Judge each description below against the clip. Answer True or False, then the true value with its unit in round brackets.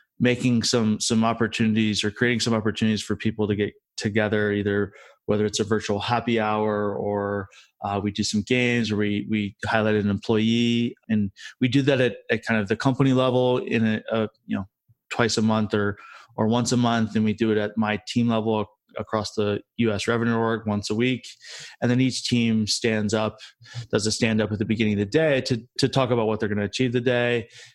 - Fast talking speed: True (215 wpm)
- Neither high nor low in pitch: False (110 Hz)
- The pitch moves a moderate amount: False (2.1 semitones)